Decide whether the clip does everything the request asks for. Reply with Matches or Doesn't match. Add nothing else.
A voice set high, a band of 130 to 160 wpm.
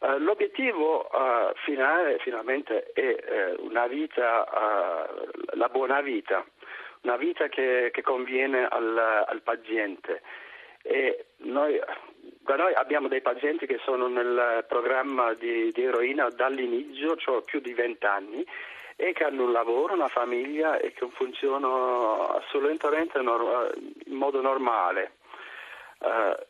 Doesn't match